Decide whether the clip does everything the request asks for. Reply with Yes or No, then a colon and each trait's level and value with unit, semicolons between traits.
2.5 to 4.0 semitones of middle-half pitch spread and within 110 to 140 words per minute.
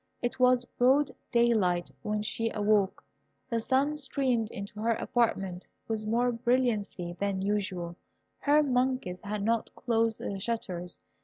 Yes: average, 3.7 semitones; slow, 135 wpm